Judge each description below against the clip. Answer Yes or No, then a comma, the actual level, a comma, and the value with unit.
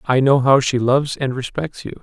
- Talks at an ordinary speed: No, fast, 235 wpm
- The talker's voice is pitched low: Yes, low, 130 Hz